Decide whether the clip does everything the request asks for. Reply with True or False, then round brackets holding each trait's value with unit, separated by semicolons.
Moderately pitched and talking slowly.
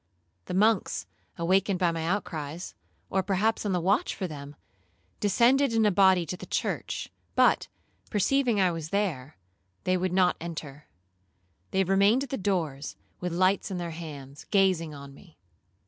False (180 Hz; 155 wpm)